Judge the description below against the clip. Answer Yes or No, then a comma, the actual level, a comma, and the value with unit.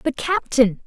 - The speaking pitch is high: Yes, very high, 260 Hz